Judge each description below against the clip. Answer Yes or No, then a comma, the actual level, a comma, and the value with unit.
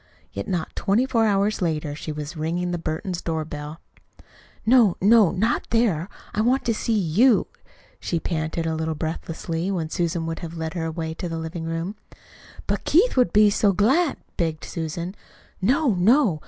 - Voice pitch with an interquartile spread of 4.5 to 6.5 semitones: Yes, average, 4.8 semitones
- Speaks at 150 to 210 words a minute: Yes, average, 175 wpm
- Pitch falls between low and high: Yes, medium, 175 Hz